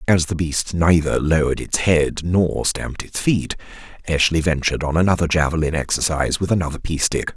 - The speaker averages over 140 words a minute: Yes, average, 170 wpm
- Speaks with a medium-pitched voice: No, very low, 80 Hz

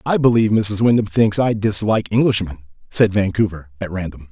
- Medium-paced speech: Yes, average, 165 wpm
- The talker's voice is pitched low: Yes, low, 105 Hz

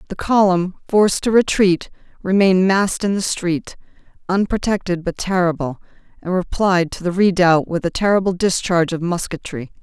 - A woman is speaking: Yes, female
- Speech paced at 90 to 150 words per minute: Yes, average, 145 wpm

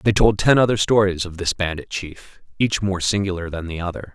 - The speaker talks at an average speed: No, fast, 215 wpm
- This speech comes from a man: Yes, male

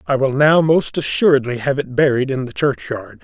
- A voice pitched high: No, medium, 140 Hz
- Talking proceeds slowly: No, fast, 205 wpm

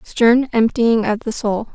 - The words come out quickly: No, average, 170 wpm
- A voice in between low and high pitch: No, high, 230 Hz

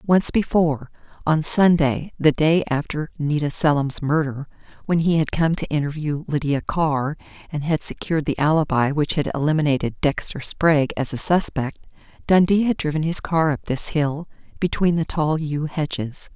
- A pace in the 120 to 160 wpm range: Yes, average, 155 wpm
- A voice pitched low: No, medium, 155 Hz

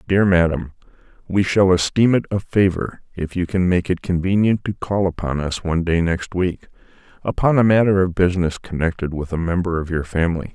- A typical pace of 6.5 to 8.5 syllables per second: No, 5.5 syllables/s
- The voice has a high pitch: No, very low, 90 Hz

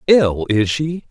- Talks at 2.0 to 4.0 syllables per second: Yes, 3.3 syllables/s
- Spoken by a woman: No, male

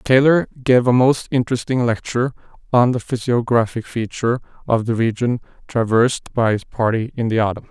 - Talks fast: No, average, 155 wpm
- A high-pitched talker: No, low, 120 Hz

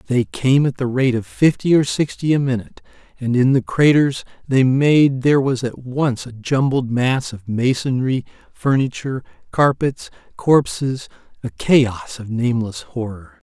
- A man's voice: Yes, male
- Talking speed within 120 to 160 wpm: Yes, average, 150 wpm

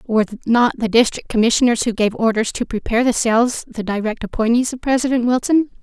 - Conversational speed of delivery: Yes, average, 185 wpm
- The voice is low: No, high, 235 Hz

